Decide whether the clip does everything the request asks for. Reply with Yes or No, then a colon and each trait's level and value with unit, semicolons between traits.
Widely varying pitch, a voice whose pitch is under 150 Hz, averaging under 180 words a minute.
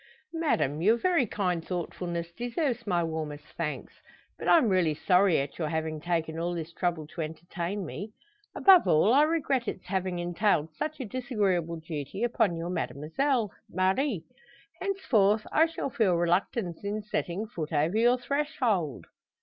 No: wide, 6.2 semitones; medium, 185 Hz; average, 150 wpm